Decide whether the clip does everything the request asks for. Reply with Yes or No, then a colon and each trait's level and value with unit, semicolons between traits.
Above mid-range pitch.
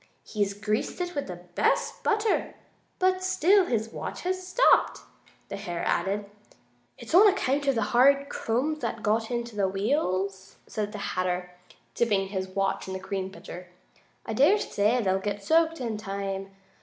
Yes: high, 215 Hz